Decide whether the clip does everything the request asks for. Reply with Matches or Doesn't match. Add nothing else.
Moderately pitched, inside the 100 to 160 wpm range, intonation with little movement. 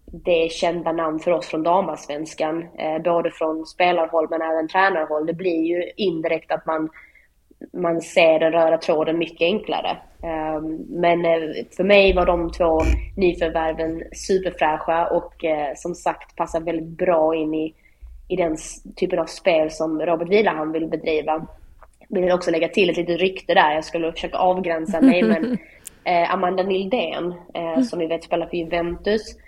Matches